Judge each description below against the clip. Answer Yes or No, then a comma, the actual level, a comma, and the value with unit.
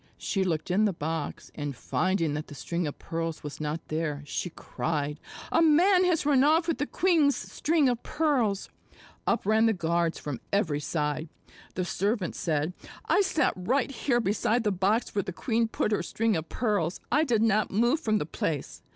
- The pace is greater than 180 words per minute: Yes, average, 190 wpm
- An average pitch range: No, wide, 7.5 semitones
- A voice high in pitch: Yes, high, 200 Hz